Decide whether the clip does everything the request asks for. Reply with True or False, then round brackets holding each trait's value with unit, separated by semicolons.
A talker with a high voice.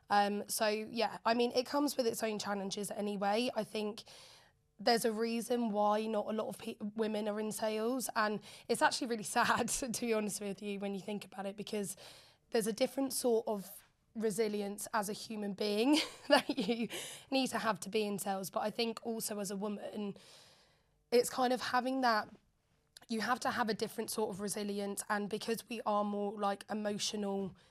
True (215 Hz)